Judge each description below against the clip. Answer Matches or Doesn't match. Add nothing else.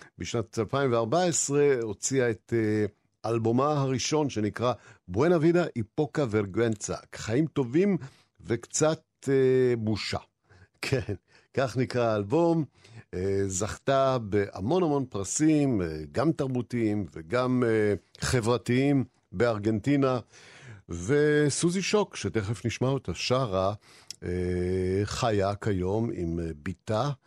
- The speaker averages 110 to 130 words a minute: Doesn't match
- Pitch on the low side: Matches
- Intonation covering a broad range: Doesn't match